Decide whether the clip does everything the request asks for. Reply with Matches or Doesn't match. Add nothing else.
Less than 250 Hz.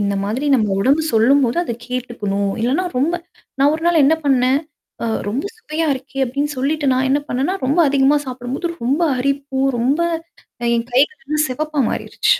Doesn't match